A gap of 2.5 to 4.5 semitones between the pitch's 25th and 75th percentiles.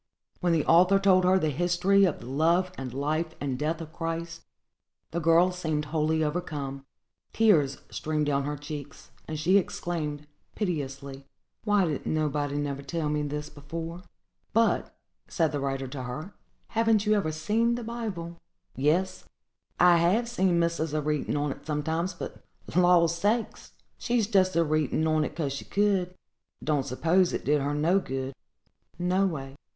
Yes: average, 3.7 semitones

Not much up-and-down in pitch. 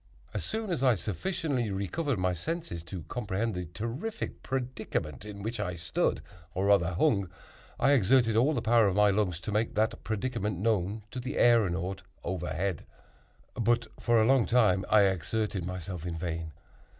No: average, 4.7 semitones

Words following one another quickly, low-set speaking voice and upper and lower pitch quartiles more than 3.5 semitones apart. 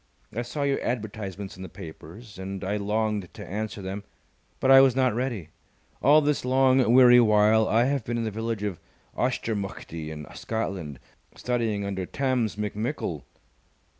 No: average, 160 wpm; low, 110 Hz; average, 4.0 semitones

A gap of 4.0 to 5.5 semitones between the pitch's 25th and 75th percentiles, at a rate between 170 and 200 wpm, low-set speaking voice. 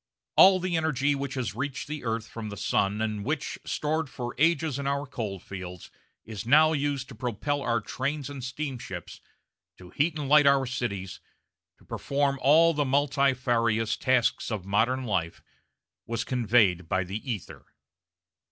No: average, 4.7 semitones; average, 160 wpm; low, 130 Hz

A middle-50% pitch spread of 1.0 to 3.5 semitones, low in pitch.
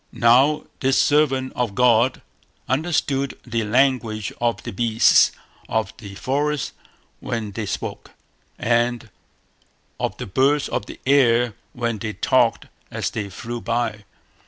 Yes: average, 3.1 semitones; low, 120 Hz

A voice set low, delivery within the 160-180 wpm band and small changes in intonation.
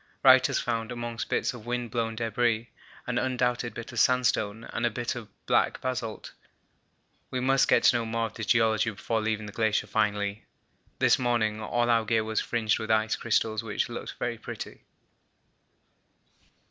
Yes: low, 115 Hz; average, 170 wpm; narrow, 1.7 semitones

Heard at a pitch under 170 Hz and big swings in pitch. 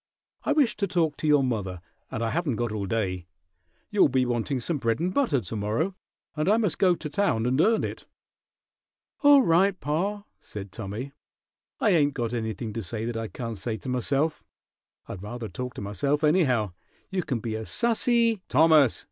Yes: low, 135 Hz; wide, 7.7 semitones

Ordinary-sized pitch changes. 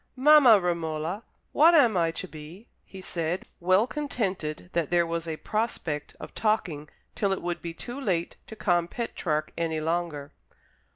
Yes: average, 4.9 semitones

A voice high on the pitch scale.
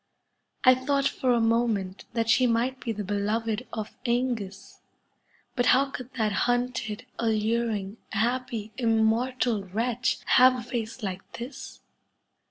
Yes: high, 230 Hz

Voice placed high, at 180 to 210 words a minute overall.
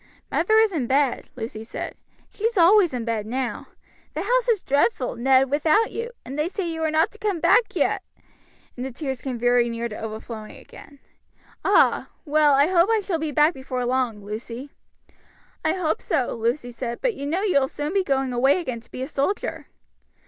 Yes: very high, 280 Hz; average, 200 wpm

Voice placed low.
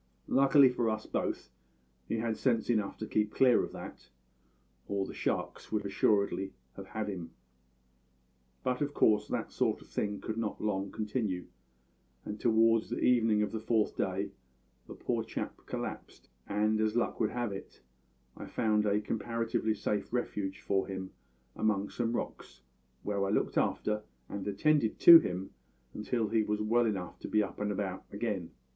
Yes: low, 105 Hz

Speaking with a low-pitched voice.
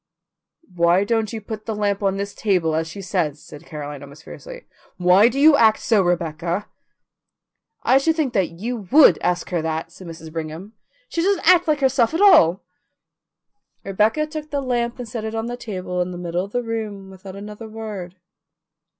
No: high, 205 Hz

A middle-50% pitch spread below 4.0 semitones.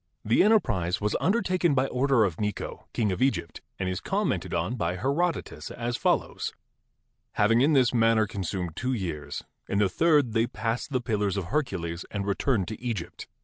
No: wide, 5.5 semitones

